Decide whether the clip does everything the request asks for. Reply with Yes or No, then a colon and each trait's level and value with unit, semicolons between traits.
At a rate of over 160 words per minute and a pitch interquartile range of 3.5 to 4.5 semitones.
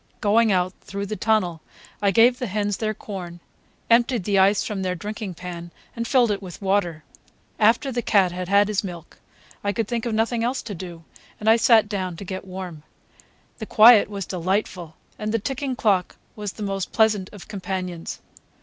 No: average, 190 wpm; average, 3.1 semitones